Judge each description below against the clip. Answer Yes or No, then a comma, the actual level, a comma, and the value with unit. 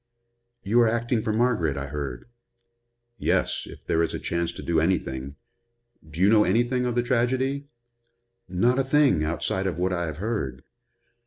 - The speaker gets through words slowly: No, average, 170 wpm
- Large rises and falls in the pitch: Yes, wide, 7.0 semitones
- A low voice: Yes, very low, 95 Hz